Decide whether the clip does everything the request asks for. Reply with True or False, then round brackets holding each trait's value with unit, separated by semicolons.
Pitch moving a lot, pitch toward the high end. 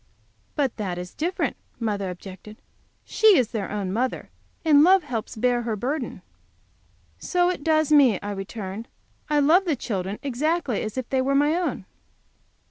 True (6.5 semitones; 250 Hz)